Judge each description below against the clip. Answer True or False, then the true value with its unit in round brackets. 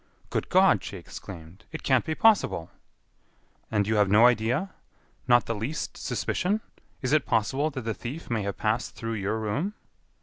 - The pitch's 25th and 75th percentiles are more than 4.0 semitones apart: True (5.5 semitones)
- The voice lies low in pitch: True (115 Hz)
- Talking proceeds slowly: False (170 wpm)